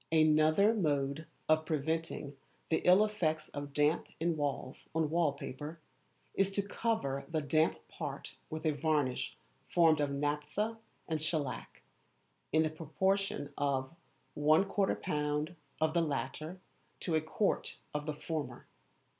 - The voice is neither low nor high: Yes, medium, 155 Hz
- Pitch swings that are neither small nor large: No, narrow, 2.2 semitones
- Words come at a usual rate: No, slow, 130 wpm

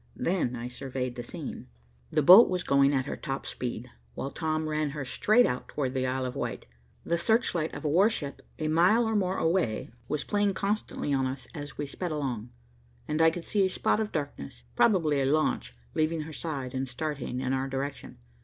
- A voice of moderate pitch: Yes, medium, 150 Hz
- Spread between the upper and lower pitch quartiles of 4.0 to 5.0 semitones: Yes, average, 4.4 semitones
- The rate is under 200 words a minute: No, fast, 205 wpm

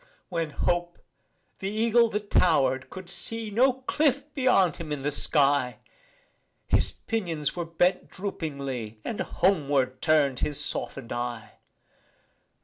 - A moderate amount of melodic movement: No, wide, 6.8 semitones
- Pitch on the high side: No, medium, 165 Hz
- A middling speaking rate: No, slow, 125 wpm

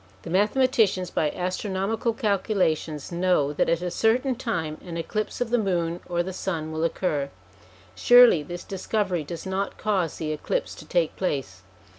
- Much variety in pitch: No, average, 4.6 semitones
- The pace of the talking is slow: No, average, 160 wpm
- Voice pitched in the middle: Yes, medium, 180 Hz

